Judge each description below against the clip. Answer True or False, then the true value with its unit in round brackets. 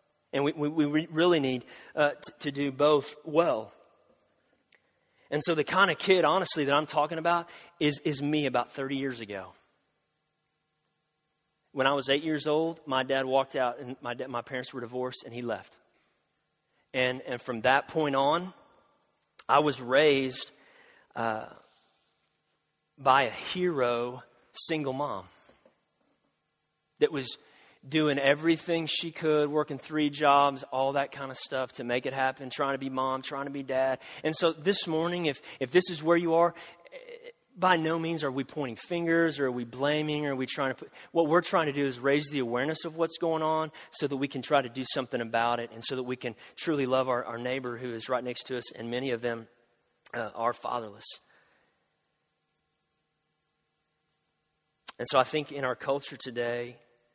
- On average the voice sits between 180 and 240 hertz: False (140 Hz)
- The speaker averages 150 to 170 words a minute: False (180 wpm)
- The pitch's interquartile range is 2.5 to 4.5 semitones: True (3.5 semitones)